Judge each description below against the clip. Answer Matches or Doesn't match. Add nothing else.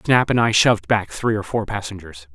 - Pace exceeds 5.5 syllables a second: Doesn't match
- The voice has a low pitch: Matches